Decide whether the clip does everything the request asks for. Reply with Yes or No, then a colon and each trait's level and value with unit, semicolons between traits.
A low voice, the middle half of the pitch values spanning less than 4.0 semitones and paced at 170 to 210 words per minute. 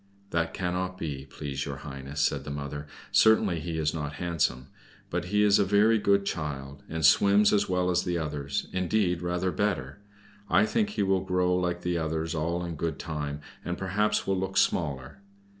No: very low, 85 Hz; average, 4.4 semitones; average, 185 wpm